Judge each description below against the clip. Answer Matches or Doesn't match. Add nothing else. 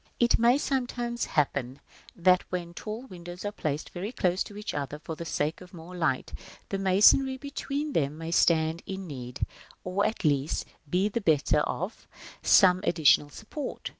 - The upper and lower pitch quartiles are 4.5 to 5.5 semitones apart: Matches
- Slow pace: Doesn't match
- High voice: Doesn't match